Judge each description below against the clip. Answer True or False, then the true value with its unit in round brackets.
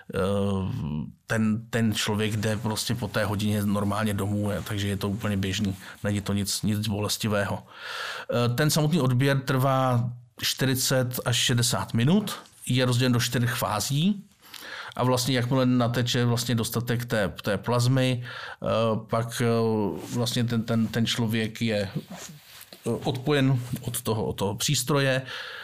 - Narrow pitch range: False (3.4 semitones)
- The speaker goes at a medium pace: True (130 wpm)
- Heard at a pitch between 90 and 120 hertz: True (115 Hz)